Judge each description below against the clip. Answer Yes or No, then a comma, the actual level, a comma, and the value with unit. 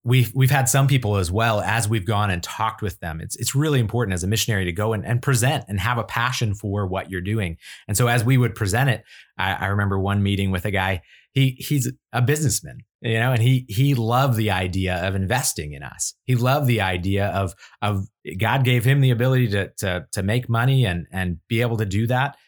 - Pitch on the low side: Yes, low, 115 Hz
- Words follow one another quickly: Yes, fast, 235 wpm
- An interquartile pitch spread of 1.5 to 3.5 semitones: No, average, 4.4 semitones